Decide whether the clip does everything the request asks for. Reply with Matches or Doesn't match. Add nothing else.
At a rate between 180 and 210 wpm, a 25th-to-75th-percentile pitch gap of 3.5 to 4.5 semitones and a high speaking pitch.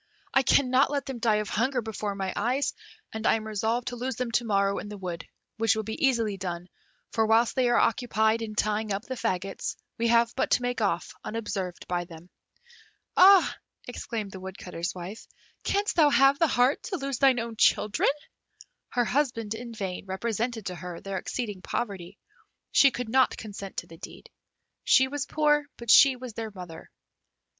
Matches